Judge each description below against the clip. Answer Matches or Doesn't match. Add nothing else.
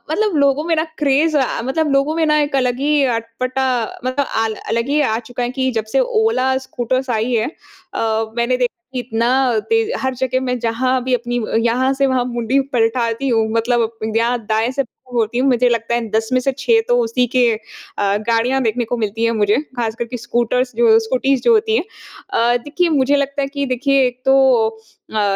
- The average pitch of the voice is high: Matches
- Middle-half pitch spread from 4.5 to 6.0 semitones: Doesn't match